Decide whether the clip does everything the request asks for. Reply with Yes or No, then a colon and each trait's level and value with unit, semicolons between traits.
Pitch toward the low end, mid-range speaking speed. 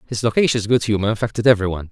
Yes: low, 110 Hz; average, 190 wpm